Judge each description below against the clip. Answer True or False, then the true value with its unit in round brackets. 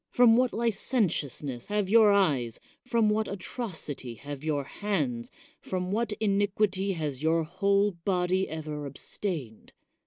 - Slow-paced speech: True (125 wpm)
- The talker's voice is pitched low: False (185 Hz)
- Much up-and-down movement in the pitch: True (5.9 semitones)